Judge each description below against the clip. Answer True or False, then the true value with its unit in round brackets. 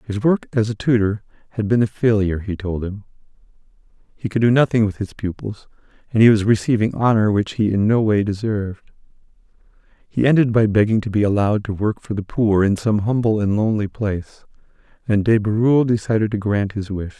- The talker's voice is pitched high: False (105 Hz)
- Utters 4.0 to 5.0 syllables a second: False (5.8 syllables/s)